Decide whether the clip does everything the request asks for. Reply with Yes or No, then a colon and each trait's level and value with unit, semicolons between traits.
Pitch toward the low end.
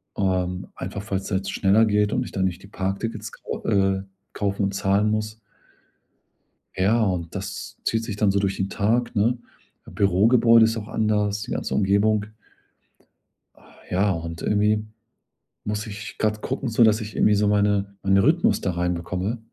Yes: low, 105 Hz